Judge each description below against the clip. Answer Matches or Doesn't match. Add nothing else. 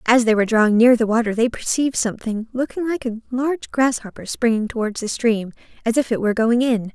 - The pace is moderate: Doesn't match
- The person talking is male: Doesn't match